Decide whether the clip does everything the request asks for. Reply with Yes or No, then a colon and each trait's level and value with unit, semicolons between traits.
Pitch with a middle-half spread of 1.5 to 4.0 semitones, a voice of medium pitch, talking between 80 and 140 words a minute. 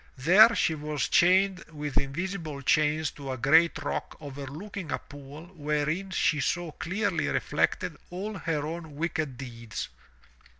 Yes: average, 3.7 semitones; medium, 155 Hz; slow, 135 wpm